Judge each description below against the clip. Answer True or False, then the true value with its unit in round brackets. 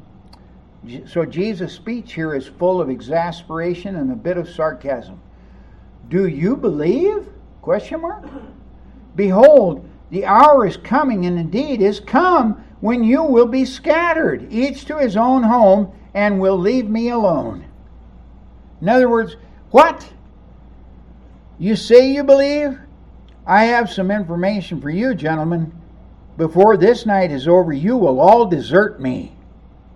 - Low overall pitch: False (195 Hz)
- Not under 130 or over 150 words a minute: True (135 wpm)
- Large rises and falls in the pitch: True (7.3 semitones)